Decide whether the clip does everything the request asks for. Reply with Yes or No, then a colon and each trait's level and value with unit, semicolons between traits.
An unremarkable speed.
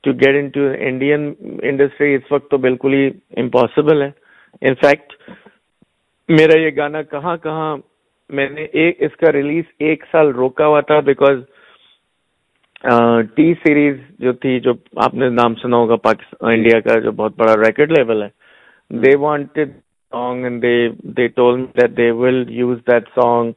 Yes: average, 120 wpm